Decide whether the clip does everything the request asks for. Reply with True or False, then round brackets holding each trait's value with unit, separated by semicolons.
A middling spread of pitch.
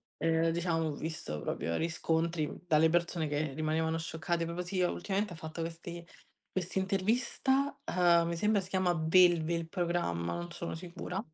False (1.8 semitones)